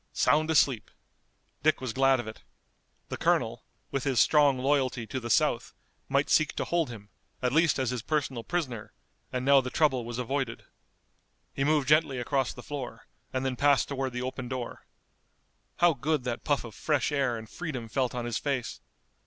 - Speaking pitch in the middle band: No, low, 130 Hz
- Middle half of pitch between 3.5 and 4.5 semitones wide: No, average, 2.9 semitones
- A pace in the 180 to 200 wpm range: Yes, average, 185 wpm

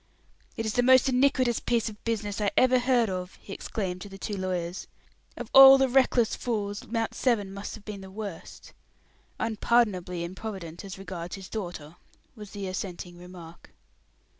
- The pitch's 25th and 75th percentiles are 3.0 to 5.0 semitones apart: Yes, average, 4.1 semitones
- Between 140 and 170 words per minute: Yes, average, 165 wpm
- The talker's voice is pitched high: Yes, high, 205 Hz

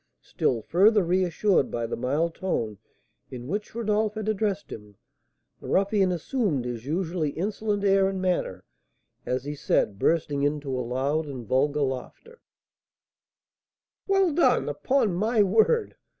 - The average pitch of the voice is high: No, medium, 175 Hz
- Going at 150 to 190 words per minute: No, slow, 135 wpm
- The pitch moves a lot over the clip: Yes, wide, 7.5 semitones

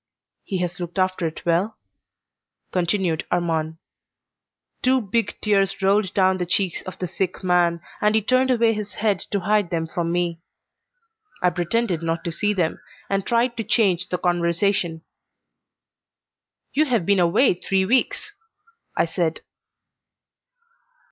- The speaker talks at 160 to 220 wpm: No, average, 140 wpm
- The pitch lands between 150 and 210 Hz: Yes, medium, 185 Hz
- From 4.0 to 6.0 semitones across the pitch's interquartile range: No, average, 3.4 semitones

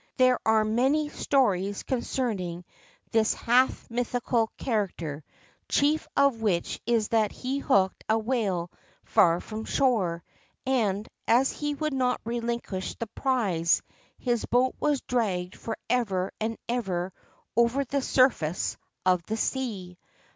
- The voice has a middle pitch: No, high, 230 Hz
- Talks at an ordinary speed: No, slow, 125 wpm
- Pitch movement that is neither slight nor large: Yes, average, 5.0 semitones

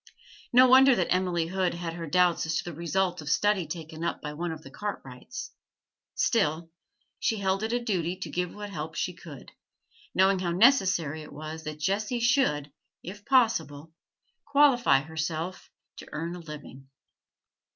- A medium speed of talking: Yes, average, 165 wpm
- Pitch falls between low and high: Yes, medium, 175 Hz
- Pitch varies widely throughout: No, average, 4.4 semitones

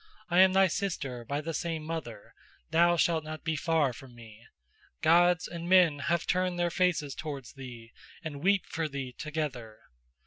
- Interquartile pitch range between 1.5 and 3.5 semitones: No, average, 4.2 semitones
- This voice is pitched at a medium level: Yes, medium, 160 Hz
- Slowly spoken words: No, average, 170 wpm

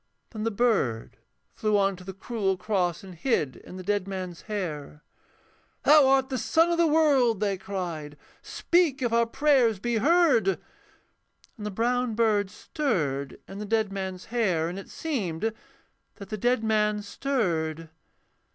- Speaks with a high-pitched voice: Yes, high, 210 Hz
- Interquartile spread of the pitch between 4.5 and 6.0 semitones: Yes, average, 4.8 semitones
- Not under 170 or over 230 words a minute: No, average, 160 wpm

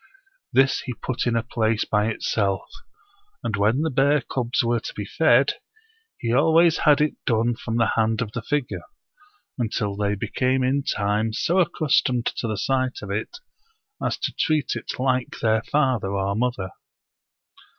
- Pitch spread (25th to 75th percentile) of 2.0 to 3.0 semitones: No, average, 3.6 semitones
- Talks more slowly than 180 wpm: Yes, average, 165 wpm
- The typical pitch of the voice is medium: No, low, 120 Hz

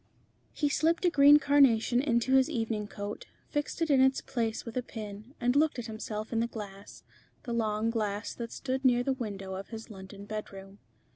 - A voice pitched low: No, high, 230 Hz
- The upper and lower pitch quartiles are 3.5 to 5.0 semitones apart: Yes, average, 4.0 semitones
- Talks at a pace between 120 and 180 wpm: No, average, 195 wpm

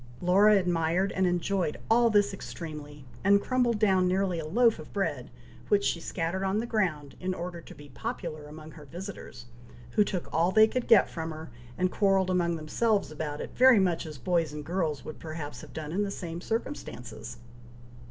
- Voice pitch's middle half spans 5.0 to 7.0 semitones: No, average, 4.4 semitones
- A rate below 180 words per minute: No, average, 190 wpm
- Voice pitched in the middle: Yes, medium, 180 Hz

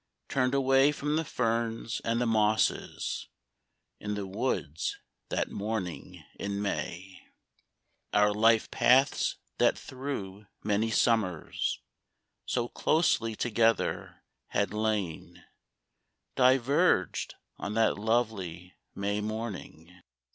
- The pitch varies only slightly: No, average, 3.2 semitones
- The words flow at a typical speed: No, slow, 95 wpm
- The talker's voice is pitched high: No, low, 110 Hz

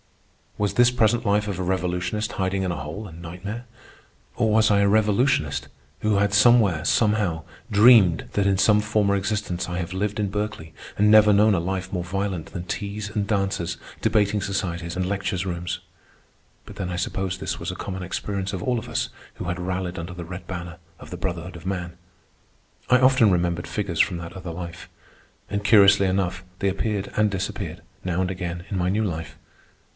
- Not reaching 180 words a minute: No, average, 190 wpm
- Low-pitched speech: Yes, very low, 95 Hz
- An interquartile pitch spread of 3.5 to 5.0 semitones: No, average, 2.9 semitones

